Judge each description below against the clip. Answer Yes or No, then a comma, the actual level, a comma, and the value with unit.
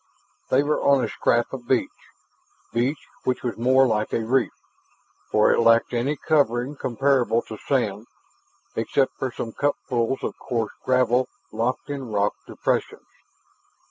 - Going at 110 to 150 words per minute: Yes, average, 140 wpm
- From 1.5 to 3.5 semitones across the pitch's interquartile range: Yes, narrow, 2.5 semitones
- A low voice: Yes, low, 125 Hz